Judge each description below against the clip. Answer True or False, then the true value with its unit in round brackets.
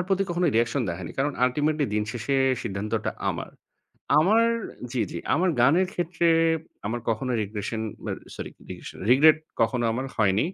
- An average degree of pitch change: False (6.1 semitones)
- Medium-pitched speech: False (125 Hz)